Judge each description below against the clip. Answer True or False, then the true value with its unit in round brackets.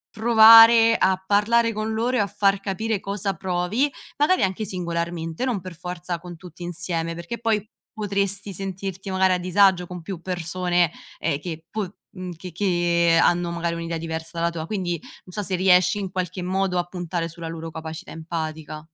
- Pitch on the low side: False (180 Hz)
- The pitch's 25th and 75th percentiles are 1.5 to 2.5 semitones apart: False (2.9 semitones)